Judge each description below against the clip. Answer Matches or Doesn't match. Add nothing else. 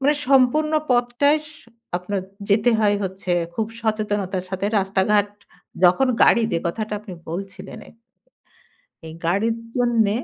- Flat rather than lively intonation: Doesn't match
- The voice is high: Matches